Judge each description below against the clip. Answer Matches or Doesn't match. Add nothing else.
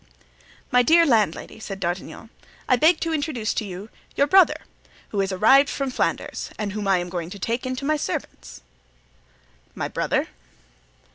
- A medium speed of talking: Matches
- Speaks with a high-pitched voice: Matches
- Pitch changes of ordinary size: Doesn't match